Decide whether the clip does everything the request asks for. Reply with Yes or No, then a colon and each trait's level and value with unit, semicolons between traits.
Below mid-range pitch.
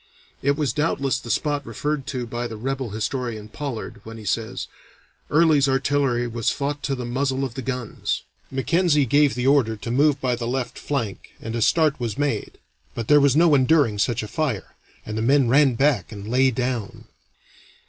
Yes: low, 130 Hz